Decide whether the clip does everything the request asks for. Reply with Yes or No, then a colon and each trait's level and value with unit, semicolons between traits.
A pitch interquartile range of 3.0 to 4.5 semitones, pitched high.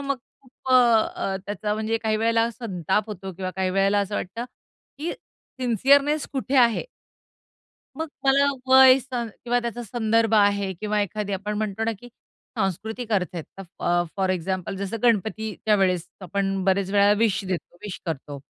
Yes: average, 3.5 semitones; high, 210 Hz